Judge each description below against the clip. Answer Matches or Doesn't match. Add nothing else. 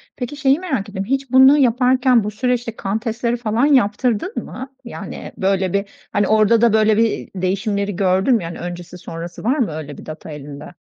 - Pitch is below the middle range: Doesn't match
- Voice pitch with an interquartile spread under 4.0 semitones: Doesn't match